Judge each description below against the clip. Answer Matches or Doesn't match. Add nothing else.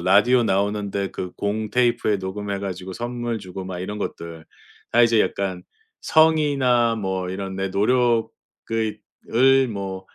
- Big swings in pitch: Doesn't match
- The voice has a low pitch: Matches